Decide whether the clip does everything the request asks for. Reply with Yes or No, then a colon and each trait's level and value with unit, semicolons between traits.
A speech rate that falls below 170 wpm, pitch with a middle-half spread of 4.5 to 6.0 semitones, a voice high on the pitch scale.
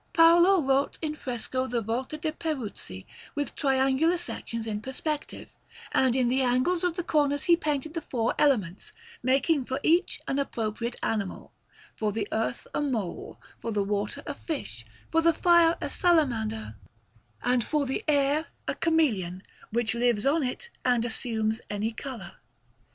Yes: average, 155 wpm; wide, 5.5 semitones; very high, 260 Hz